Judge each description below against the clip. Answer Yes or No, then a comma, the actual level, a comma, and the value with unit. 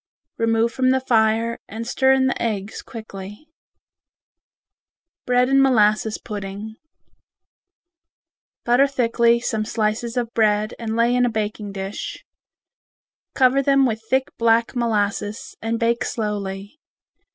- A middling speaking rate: No, slow, 120 wpm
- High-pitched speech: Yes, high, 230 Hz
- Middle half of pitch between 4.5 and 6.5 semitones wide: No, narrow, 2.6 semitones